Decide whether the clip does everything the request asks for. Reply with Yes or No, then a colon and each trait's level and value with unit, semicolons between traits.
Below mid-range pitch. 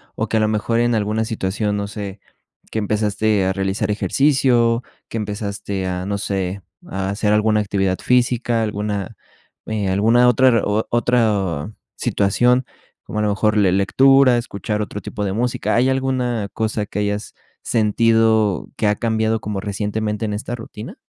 Yes: low, 105 Hz